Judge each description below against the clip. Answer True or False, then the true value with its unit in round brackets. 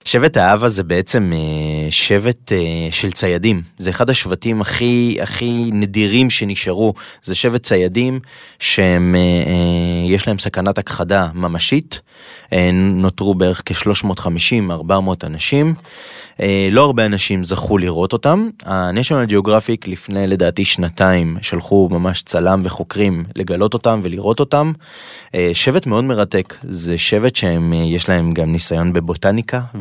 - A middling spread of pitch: True (4.0 semitones)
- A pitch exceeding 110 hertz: False (95 Hz)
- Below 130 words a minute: True (110 wpm)